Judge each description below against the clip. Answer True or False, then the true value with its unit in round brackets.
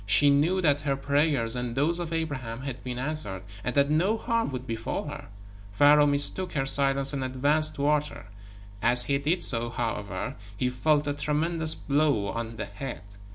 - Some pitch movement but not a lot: True (3.4 semitones)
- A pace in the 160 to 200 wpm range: True (180 wpm)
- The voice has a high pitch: False (140 Hz)